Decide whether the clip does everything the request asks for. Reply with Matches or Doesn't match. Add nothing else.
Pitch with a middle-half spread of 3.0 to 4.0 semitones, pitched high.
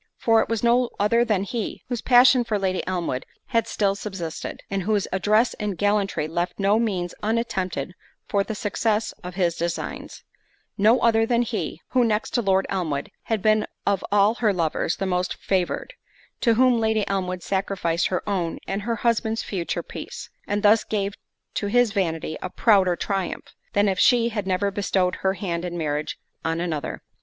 Matches